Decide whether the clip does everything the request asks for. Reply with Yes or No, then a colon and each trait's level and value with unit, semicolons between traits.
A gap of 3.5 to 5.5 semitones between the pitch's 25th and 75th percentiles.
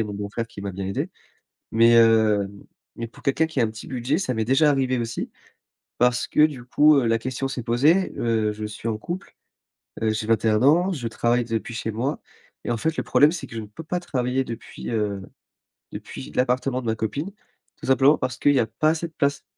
Yes: average, 4.0 semitones